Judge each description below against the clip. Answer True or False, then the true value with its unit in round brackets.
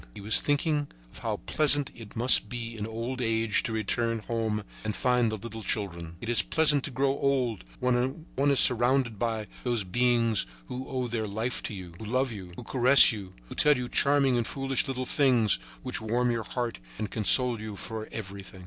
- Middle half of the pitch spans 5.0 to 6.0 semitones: False (3.0 semitones)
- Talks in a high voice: False (120 Hz)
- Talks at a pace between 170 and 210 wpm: True (200 wpm)